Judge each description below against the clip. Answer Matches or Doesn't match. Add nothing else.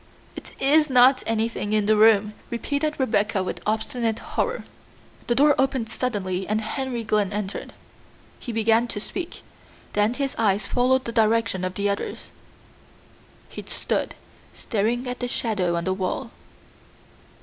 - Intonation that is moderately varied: Matches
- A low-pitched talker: Doesn't match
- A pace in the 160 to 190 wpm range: Doesn't match